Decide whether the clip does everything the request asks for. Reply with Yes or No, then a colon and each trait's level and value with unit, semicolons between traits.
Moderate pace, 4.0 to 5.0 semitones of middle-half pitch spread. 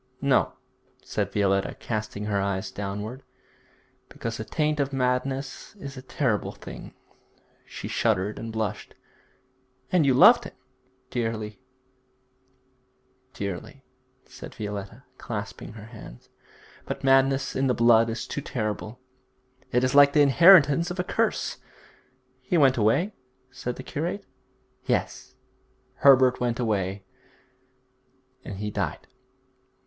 No: slow, 120 wpm; average, 4.6 semitones